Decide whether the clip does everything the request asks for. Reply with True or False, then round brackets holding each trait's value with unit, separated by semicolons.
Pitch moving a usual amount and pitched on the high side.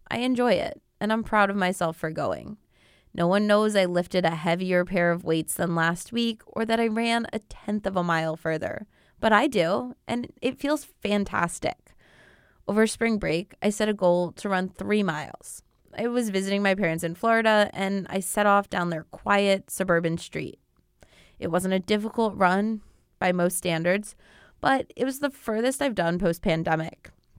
True (4.3 semitones; 195 Hz)